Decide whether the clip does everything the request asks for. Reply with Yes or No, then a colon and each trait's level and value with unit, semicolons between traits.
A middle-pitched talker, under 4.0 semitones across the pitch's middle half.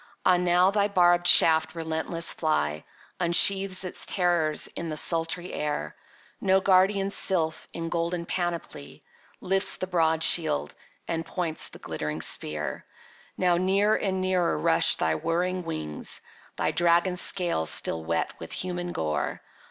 Yes: medium, 175 Hz; narrow, 2.6 semitones